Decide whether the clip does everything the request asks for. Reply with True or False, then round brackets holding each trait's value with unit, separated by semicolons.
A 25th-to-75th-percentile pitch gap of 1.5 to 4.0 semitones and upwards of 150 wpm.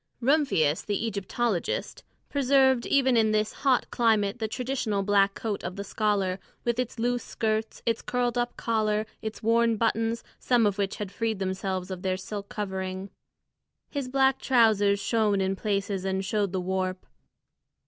True (3.4 semitones; 160 wpm)